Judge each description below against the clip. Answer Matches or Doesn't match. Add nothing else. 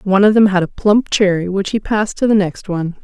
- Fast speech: Matches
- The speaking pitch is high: Matches